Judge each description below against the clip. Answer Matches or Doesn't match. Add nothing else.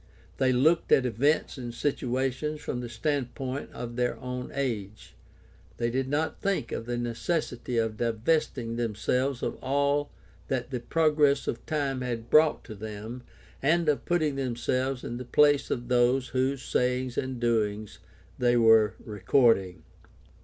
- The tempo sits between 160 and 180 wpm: Doesn't match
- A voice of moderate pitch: Doesn't match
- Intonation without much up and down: Doesn't match